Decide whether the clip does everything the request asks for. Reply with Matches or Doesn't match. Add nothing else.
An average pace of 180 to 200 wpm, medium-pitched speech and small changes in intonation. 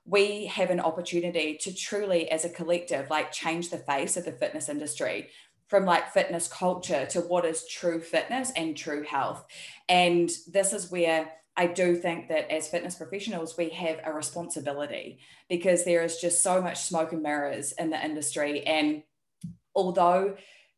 Doesn't match